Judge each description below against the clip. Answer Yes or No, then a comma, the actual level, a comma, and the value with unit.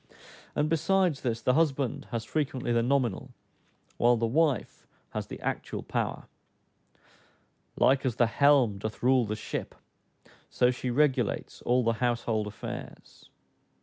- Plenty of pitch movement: No, average, 3.3 semitones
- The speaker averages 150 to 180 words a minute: No, slow, 135 wpm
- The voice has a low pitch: Yes, low, 125 Hz